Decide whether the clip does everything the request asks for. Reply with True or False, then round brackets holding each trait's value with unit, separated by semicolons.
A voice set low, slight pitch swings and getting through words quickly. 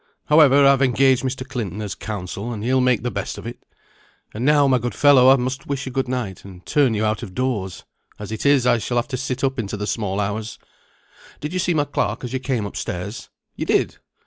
False (125 Hz; 3.9 semitones; 235 wpm)